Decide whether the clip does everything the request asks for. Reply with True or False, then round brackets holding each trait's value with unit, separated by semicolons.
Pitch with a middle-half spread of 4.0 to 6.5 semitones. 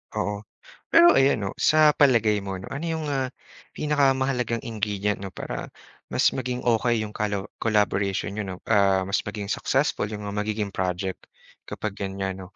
True (4.4 semitones)